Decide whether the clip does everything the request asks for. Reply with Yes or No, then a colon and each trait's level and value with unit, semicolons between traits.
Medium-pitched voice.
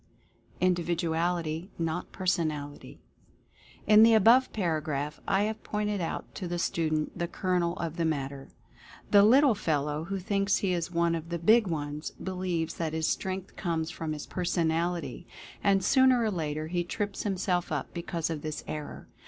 Yes: medium, 170 Hz